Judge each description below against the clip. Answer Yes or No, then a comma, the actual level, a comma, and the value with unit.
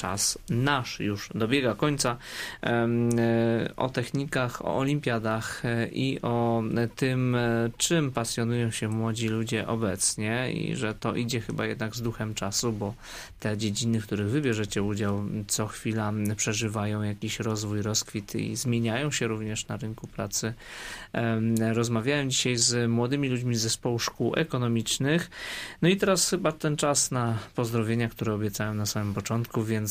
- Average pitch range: No, narrow, 2.3 semitones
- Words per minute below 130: No, average, 140 wpm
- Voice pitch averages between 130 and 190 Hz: No, low, 115 Hz